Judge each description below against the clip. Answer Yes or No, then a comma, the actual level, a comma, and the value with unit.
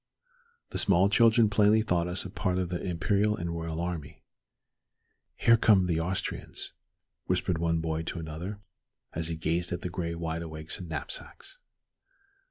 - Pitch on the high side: No, very low, 85 Hz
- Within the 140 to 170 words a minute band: Yes, average, 160 wpm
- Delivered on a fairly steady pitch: No, average, 3.1 semitones